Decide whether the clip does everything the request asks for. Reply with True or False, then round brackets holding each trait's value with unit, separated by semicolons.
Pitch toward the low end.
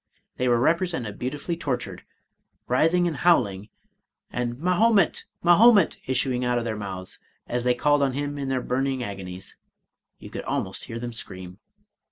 True (125 Hz)